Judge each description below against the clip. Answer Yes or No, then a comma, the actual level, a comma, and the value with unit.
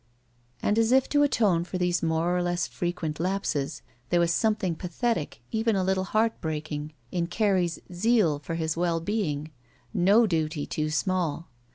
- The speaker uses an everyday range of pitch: Yes, average, 4.0 semitones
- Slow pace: No, average, 160 wpm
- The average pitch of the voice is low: No, medium, 175 Hz